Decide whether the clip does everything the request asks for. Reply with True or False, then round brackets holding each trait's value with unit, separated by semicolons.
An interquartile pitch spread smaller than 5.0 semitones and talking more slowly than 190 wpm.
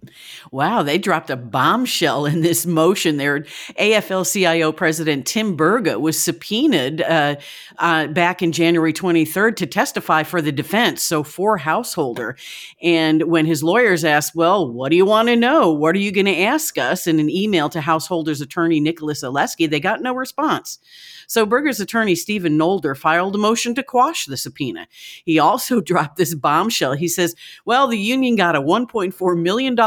False (5.3 semitones; 175 wpm)